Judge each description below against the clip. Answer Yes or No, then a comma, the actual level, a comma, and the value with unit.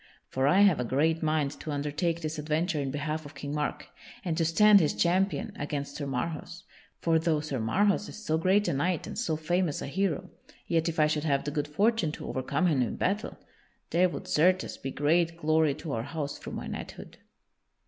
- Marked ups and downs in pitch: No, average, 3.2 semitones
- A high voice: No, medium, 155 Hz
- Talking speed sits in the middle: No, fast, 210 wpm